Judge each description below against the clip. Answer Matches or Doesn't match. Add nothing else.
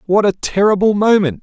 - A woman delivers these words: Doesn't match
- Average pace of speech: Matches